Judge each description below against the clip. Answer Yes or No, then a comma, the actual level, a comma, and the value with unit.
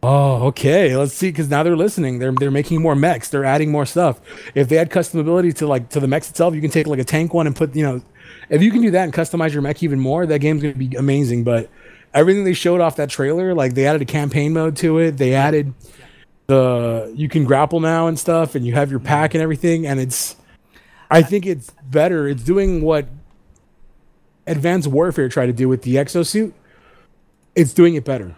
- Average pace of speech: No, fast, 225 wpm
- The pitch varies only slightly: No, average, 3.5 semitones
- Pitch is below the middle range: No, medium, 150 Hz